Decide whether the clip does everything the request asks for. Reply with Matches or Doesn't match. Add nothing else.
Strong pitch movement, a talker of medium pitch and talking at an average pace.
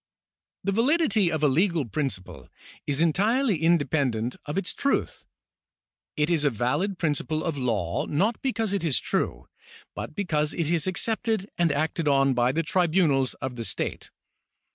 Matches